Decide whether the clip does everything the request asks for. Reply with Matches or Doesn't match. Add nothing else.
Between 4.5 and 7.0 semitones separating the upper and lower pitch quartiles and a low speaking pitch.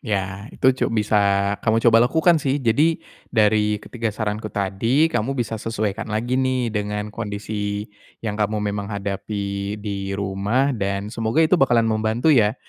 Doesn't match